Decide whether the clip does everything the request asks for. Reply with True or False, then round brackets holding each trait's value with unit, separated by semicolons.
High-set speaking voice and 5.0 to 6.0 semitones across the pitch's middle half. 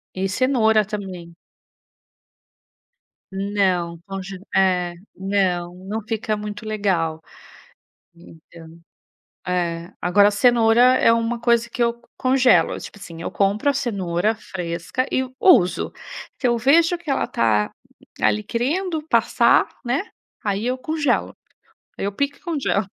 True (205 Hz; 5.3 semitones)